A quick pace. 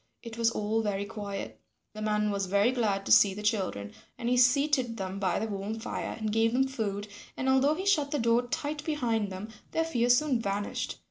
Yes: fast, 210 wpm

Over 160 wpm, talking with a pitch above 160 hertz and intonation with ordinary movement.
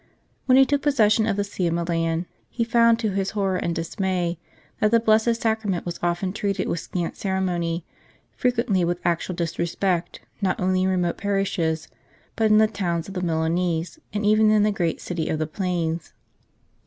Yes: average, 180 wpm; medium, 185 Hz; average, 3.8 semitones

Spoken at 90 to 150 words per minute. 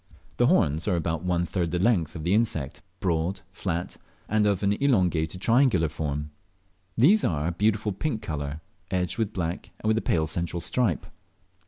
No: average, 180 wpm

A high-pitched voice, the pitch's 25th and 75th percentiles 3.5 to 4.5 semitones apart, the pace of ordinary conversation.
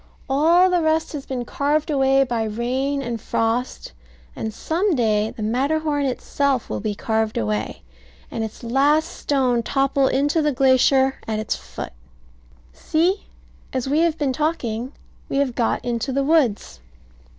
Yes: very high, 270 Hz; average, 4.1 semitones; average, 150 wpm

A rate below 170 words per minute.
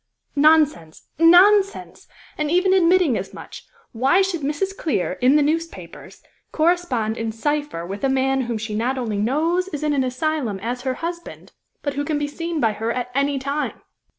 No: average, 180 wpm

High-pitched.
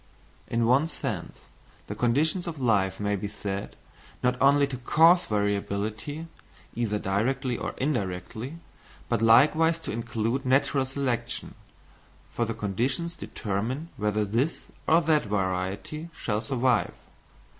No: low, 120 Hz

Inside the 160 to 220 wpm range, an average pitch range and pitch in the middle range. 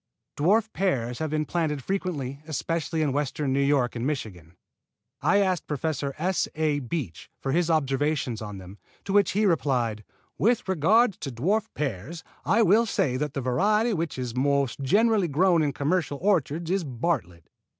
No: average, 165 wpm; wide, 5.7 semitones; medium, 150 Hz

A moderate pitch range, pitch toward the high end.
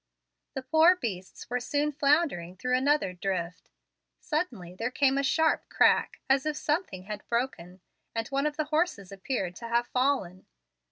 No: wide, 7.6 semitones; very high, 255 Hz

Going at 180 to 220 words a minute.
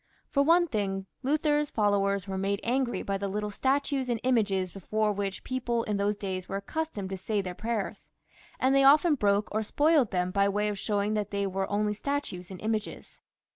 Yes: average, 195 wpm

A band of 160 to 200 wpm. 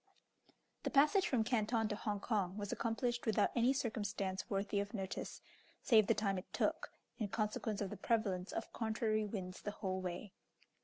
Yes: average, 170 wpm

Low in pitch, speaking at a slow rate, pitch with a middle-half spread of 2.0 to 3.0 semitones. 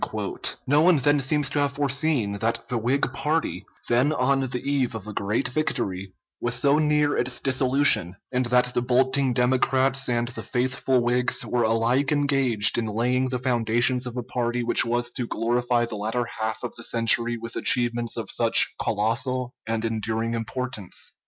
No: low, 125 Hz; average, 170 wpm; narrow, 2.5 semitones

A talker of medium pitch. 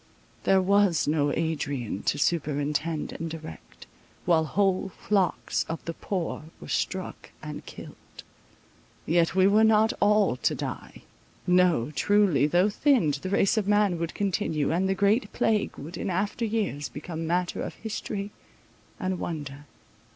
Yes: medium, 175 Hz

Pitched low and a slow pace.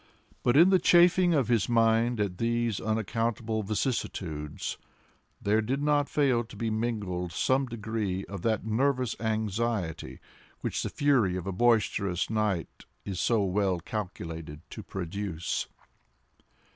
Yes: low, 110 Hz; slow, 130 wpm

